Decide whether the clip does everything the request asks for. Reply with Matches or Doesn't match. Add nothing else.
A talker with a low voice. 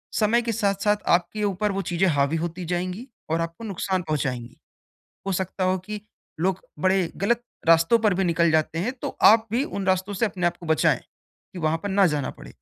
Doesn't match